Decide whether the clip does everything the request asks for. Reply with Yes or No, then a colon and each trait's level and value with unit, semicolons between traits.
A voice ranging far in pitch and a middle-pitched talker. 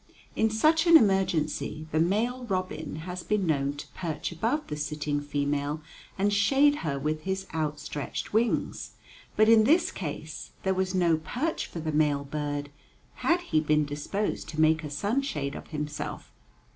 Yes: wide, 6.0 semitones; medium, 160 Hz